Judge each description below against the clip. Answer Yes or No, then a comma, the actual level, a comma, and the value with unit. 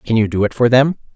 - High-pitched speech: No, low, 120 Hz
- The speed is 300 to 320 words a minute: Yes, fast, 315 wpm